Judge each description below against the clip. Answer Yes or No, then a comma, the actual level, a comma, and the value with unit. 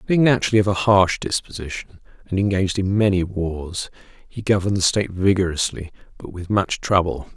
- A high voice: No, very low, 95 Hz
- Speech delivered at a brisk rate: No, average, 165 wpm